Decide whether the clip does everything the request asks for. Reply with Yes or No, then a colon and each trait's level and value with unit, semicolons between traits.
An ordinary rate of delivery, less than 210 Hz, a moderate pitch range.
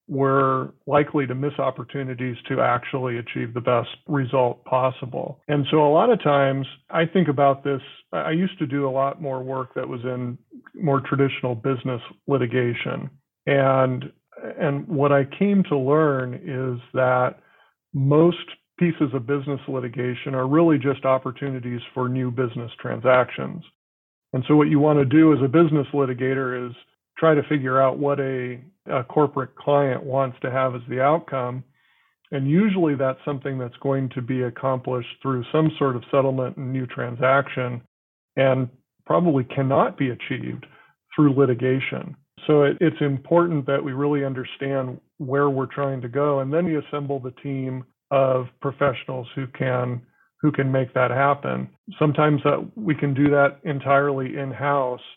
No: average, 160 wpm; low, 135 Hz; narrow, 2.1 semitones